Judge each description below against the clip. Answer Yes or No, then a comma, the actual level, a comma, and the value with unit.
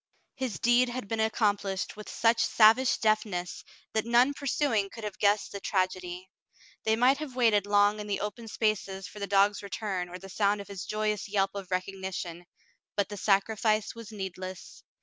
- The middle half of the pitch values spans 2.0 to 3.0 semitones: Yes, narrow, 2.4 semitones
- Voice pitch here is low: No, high, 205 Hz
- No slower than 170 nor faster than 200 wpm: Yes, average, 185 wpm